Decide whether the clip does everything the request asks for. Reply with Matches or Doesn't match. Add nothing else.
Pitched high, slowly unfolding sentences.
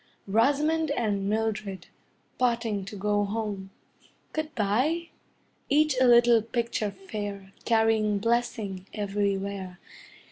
Matches